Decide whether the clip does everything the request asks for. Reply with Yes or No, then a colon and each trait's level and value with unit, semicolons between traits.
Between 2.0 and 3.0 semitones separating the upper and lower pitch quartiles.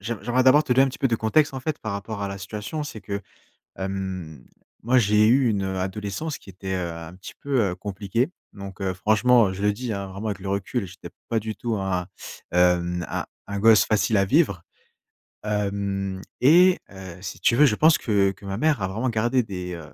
No: average, 3.8 semitones